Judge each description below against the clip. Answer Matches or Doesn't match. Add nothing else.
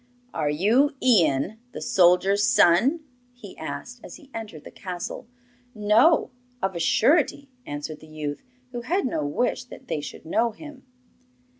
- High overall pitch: Matches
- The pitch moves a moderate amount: Doesn't match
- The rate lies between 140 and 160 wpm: Matches